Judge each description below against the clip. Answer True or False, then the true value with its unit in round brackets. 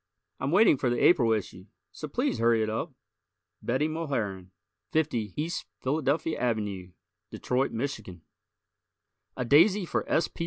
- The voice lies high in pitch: False (130 Hz)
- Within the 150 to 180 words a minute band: False (140 wpm)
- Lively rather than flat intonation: True (5.9 semitones)